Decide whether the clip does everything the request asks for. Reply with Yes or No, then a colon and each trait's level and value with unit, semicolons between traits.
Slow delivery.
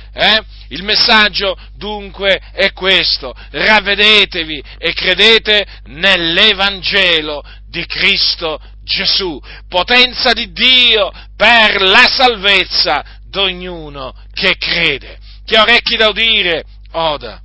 Yes: slow, 95 wpm